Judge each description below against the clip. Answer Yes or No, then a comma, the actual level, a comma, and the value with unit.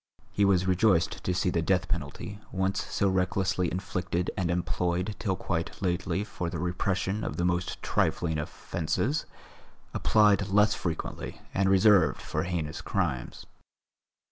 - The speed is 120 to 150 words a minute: Yes, average, 140 wpm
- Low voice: Yes, very low, 90 Hz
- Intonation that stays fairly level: Yes, narrow, 2.0 semitones